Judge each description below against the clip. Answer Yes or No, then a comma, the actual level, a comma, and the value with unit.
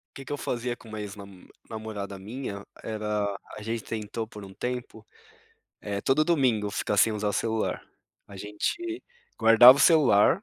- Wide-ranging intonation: No, average, 3.3 semitones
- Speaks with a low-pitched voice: Yes, low, 110 Hz